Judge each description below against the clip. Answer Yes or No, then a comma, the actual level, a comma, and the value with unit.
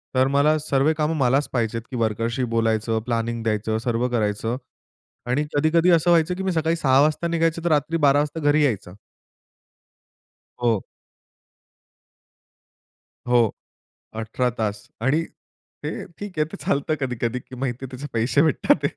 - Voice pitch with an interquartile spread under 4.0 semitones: No, average, 5.1 semitones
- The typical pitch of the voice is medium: No, low, 130 Hz